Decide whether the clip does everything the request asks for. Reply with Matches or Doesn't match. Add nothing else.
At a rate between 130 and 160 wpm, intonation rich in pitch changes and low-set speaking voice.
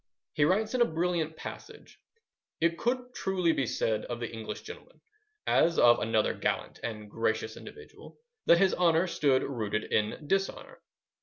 Doesn't match